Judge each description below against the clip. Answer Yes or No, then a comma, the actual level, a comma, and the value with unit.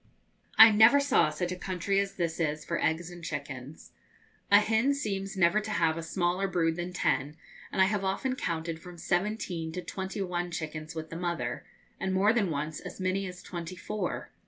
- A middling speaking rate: Yes, average, 195 wpm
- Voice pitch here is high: No, medium, 180 Hz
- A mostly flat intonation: No, average, 3.2 semitones